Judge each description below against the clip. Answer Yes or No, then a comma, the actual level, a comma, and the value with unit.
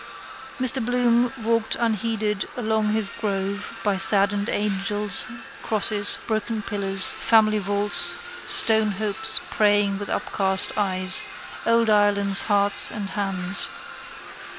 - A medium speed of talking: No, slow, 105 wpm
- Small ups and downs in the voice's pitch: Yes, narrow, 1.7 semitones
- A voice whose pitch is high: Yes, high, 205 Hz